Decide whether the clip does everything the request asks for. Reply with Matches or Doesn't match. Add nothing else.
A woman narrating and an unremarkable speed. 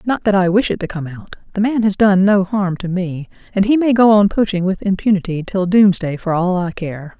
Doesn't match